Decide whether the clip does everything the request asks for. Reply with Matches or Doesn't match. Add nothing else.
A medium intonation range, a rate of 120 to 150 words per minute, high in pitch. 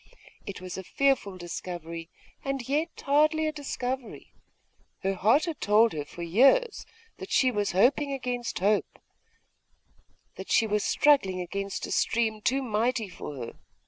Doesn't match